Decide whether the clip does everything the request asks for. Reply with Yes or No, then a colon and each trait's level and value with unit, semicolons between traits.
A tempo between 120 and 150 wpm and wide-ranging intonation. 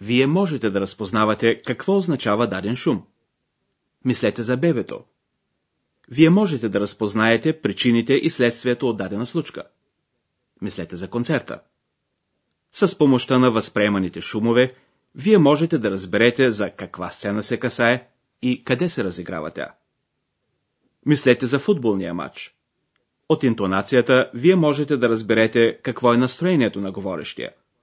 No: average, 125 wpm; average, 4.7 semitones